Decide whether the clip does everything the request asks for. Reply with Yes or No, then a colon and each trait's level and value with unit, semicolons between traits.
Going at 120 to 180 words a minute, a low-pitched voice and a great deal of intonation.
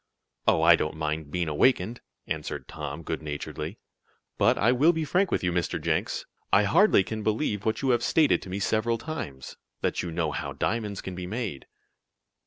No: average, 190 wpm; low, 100 Hz; wide, 6.7 semitones